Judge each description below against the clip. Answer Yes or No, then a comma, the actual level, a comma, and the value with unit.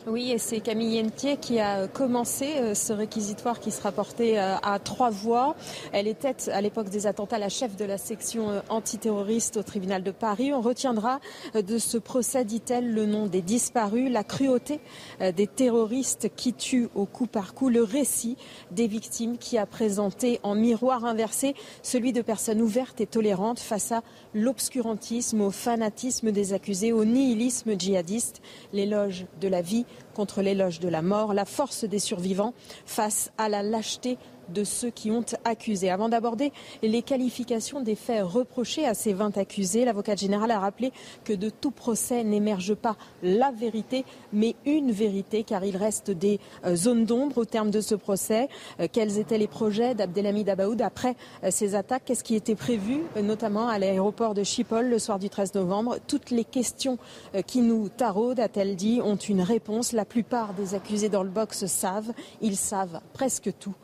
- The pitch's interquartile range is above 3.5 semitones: No, average, 2.7 semitones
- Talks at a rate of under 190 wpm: Yes, average, 170 wpm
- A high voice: Yes, high, 220 Hz